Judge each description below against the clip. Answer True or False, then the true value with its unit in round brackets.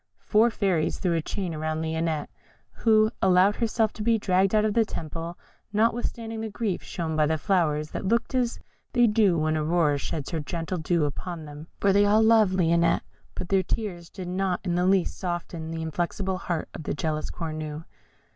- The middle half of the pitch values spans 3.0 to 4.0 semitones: False (4.6 semitones)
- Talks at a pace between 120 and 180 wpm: False (190 wpm)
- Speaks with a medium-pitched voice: True (180 Hz)